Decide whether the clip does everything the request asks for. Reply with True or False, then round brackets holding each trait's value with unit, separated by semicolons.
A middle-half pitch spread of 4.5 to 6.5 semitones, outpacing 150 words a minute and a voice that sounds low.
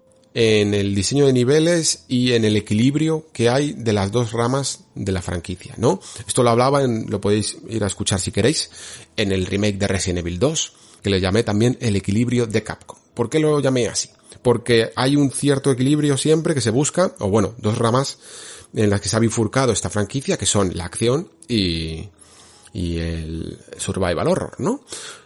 True (4.9 semitones; 190 wpm; 115 Hz)